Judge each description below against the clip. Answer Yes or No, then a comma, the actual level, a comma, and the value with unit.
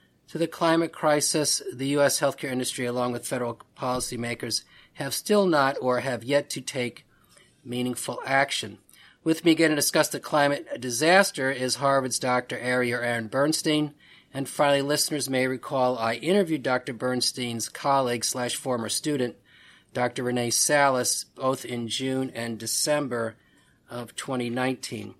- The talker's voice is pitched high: No, low, 130 Hz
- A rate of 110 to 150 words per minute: Yes, average, 140 wpm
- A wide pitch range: No, average, 3.1 semitones